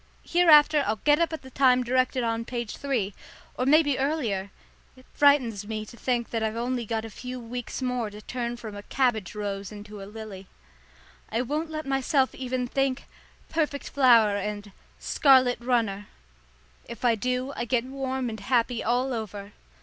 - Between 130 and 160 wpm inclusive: No, average, 175 wpm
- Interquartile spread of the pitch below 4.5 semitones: Yes, average, 3.4 semitones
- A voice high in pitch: Yes, high, 245 Hz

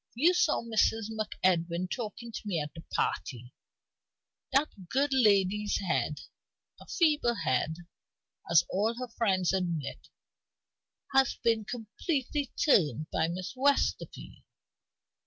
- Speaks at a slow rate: Yes, slow, 115 wpm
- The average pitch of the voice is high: Yes, high, 210 Hz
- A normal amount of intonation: No, wide, 6.4 semitones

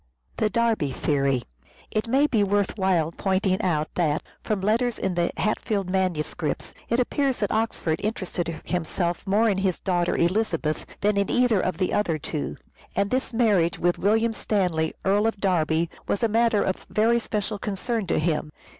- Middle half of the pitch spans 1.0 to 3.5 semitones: No, average, 4.1 semitones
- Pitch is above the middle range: Yes, high, 195 Hz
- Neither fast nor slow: Yes, average, 165 wpm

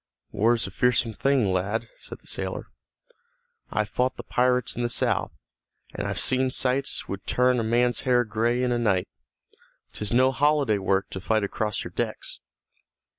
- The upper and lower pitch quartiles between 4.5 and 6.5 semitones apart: No, average, 2.9 semitones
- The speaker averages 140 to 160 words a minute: No, average, 170 wpm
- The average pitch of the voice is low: Yes, low, 120 Hz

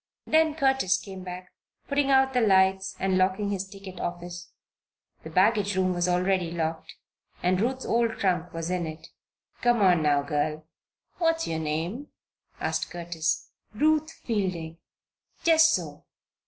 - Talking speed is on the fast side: No, average, 140 wpm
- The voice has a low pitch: No, medium, 185 Hz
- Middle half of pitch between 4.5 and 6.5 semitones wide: Yes, average, 5.2 semitones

